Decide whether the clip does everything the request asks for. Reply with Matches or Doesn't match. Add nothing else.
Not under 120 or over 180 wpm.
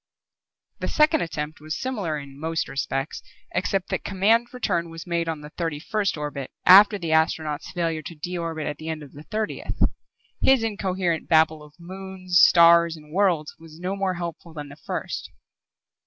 Matches